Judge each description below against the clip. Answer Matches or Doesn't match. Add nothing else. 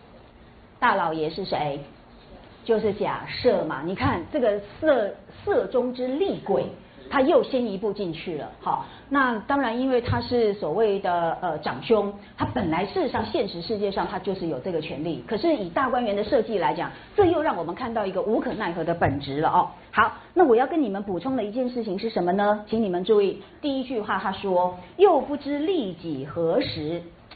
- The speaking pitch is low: Doesn't match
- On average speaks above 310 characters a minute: Doesn't match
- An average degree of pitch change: Doesn't match